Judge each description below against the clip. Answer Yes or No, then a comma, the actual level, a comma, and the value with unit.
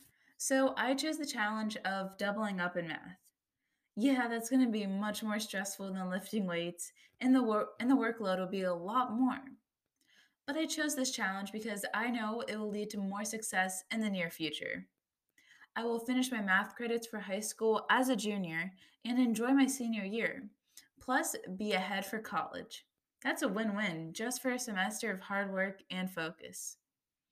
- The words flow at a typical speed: Yes, average, 185 wpm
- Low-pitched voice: No, high, 215 Hz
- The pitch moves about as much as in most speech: Yes, average, 4.4 semitones